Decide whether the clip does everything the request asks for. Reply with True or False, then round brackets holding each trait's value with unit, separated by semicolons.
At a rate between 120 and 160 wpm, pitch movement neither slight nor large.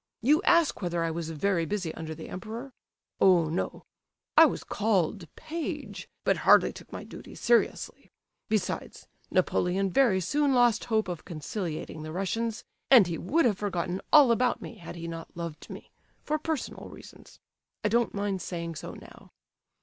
False (155 wpm; 5.9 semitones)